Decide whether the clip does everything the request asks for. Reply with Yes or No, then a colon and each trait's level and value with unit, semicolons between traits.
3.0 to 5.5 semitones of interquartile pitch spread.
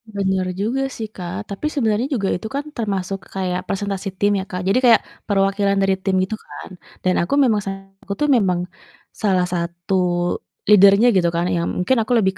No: narrow, 2.4 semitones